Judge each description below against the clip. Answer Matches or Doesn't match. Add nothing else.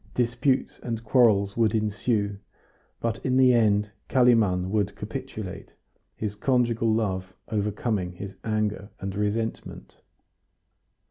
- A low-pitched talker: Matches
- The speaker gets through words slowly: Matches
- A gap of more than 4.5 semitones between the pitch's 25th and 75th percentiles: Doesn't match